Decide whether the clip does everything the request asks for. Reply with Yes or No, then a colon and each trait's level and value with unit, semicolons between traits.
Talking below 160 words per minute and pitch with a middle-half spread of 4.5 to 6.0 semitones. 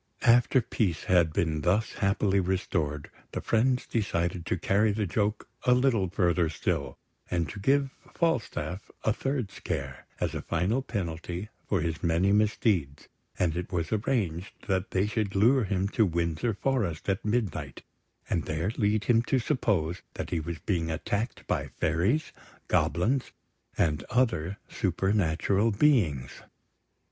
Yes: average, 145 wpm; average, 4.9 semitones